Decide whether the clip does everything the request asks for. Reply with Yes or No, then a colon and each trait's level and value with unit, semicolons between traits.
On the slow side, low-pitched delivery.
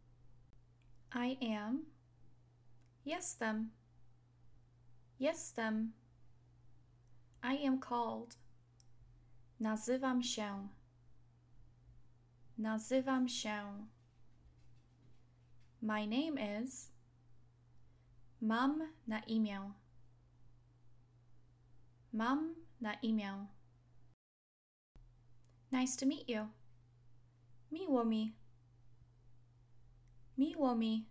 Yes: slow, 60 wpm; low, 120 Hz